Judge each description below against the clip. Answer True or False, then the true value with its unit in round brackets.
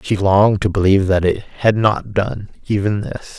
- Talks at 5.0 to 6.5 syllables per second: False (4.8 syllables/s)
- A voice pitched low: True (100 Hz)